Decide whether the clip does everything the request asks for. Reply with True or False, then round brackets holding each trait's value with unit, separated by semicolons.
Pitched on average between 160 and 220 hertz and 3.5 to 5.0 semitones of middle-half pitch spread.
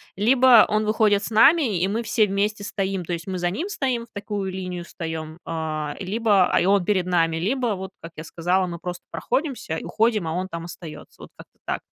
True (190 Hz; 4.1 semitones)